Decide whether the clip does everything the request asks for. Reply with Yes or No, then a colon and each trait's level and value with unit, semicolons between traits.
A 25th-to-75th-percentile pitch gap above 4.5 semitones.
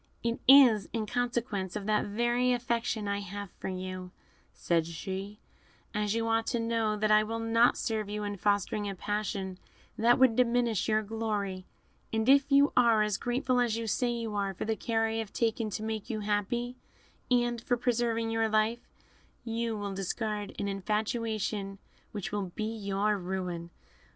No: narrow, 2.4 semitones